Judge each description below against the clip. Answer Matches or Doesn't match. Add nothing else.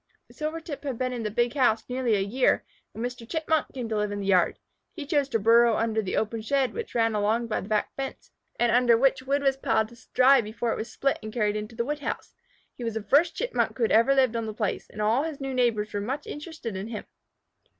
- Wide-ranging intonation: Doesn't match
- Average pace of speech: Doesn't match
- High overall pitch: Matches